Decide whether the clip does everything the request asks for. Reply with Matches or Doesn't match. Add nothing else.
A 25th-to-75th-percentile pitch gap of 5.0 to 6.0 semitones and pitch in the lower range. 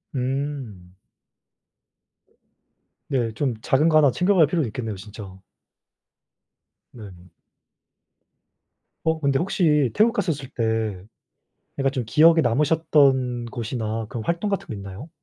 Matches